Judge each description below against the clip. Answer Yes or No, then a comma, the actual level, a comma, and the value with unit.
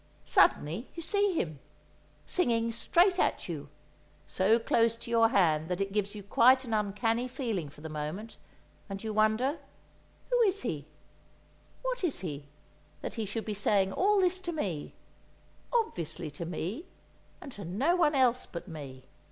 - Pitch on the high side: Yes, high, 220 Hz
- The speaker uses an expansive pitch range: Yes, wide, 7.6 semitones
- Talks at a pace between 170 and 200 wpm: No, average, 155 wpm